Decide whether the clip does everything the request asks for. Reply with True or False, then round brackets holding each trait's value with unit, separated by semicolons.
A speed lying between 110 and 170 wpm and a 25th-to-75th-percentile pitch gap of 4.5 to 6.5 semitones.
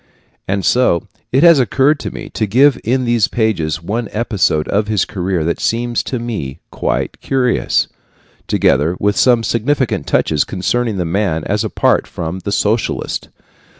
True (155 wpm; 5.1 semitones)